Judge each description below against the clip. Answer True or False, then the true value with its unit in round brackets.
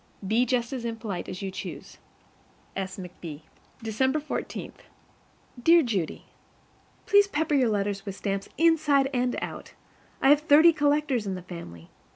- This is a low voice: False (235 Hz)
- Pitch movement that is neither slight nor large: False (7.0 semitones)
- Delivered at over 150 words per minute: False (145 wpm)